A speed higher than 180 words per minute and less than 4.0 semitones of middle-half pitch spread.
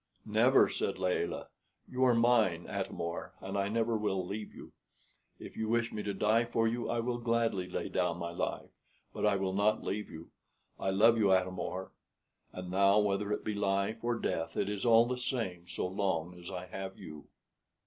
Yes: average, 200 wpm; average, 3.5 semitones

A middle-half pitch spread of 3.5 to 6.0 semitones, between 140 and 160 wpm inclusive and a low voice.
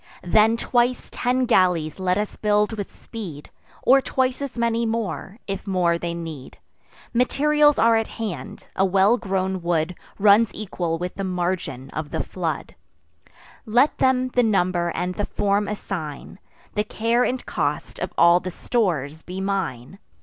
No: average, 4.7 semitones; average, 155 wpm; high, 195 Hz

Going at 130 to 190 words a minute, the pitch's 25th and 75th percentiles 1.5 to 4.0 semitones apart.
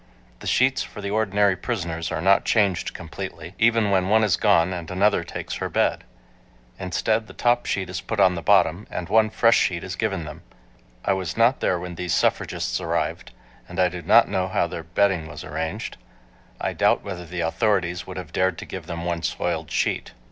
No: average, 200 wpm; average, 3.2 semitones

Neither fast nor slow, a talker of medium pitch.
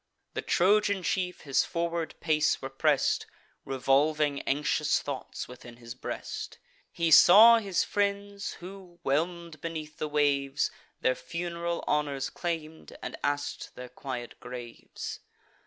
No: slow, 120 wpm; medium, 155 Hz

